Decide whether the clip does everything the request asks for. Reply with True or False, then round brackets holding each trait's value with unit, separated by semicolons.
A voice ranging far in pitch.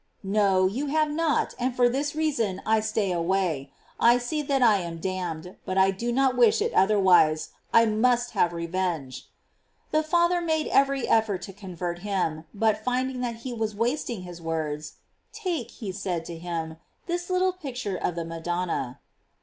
True (6.9 semitones)